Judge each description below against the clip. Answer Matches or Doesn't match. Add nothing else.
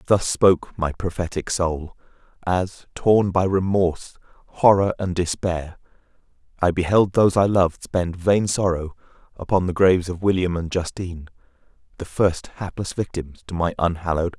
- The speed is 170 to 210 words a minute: Doesn't match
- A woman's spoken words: Doesn't match